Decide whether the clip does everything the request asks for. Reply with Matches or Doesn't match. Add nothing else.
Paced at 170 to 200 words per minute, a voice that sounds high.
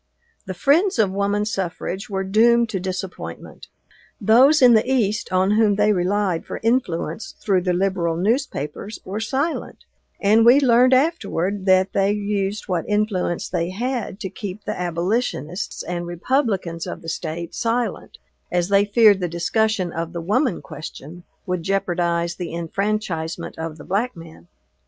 Doesn't match